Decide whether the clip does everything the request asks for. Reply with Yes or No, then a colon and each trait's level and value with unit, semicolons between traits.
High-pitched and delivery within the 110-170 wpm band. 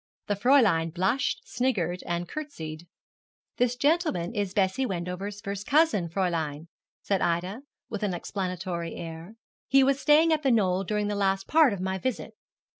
Yes: high, 195 Hz; average, 155 wpm